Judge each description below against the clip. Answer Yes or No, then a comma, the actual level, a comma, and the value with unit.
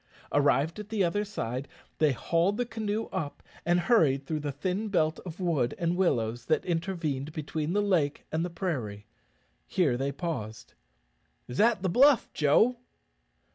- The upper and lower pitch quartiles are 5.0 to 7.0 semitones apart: Yes, wide, 5.4 semitones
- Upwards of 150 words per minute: Yes, average, 160 wpm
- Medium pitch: Yes, medium, 165 Hz